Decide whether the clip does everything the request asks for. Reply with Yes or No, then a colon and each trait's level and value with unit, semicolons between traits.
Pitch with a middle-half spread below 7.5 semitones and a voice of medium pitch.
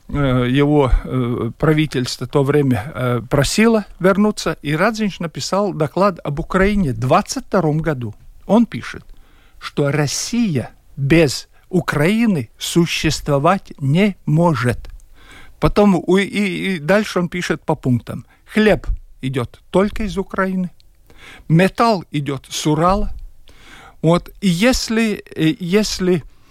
Yes: wide, 5.5 semitones; medium, 170 Hz